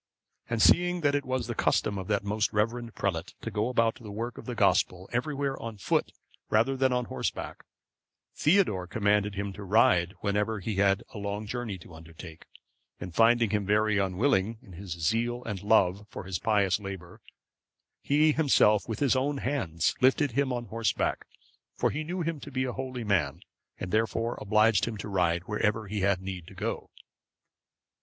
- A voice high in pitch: No, low, 105 Hz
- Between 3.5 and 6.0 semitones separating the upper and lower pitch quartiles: Yes, average, 4.0 semitones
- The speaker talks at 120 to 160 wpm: No, average, 180 wpm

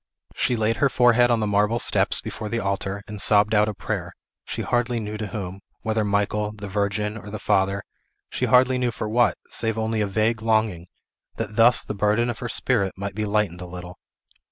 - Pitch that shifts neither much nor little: No, narrow, 2.1 semitones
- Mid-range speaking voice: No, low, 105 Hz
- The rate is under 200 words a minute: No, fast, 205 wpm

